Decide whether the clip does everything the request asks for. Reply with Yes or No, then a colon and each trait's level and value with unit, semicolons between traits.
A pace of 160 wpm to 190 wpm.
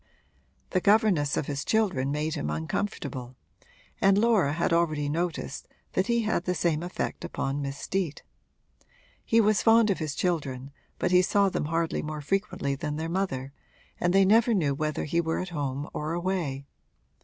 Yes: average, 170 wpm